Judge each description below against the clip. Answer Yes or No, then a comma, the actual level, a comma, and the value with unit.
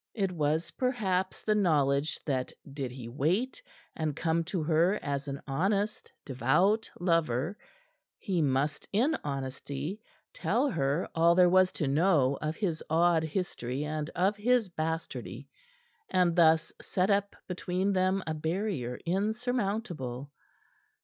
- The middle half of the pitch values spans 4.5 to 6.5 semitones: Yes, average, 5.1 semitones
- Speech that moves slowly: Yes, slow, 130 wpm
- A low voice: No, medium, 170 Hz